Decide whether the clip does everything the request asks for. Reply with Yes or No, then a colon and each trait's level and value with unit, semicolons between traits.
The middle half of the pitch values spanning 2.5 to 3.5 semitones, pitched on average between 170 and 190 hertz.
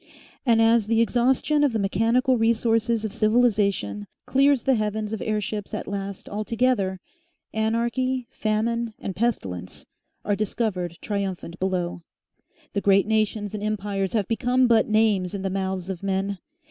No: average, 3.0 semitones; high, 215 Hz